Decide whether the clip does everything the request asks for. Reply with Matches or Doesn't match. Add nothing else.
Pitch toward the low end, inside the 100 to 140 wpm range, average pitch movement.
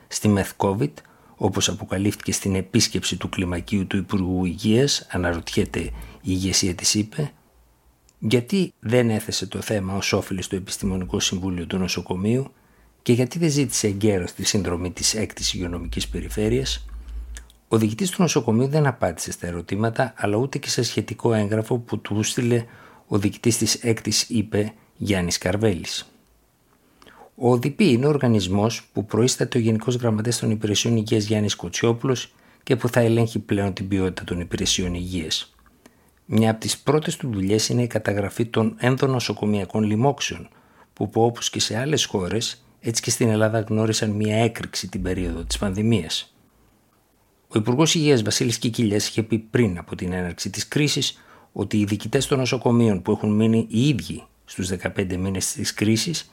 Doesn't match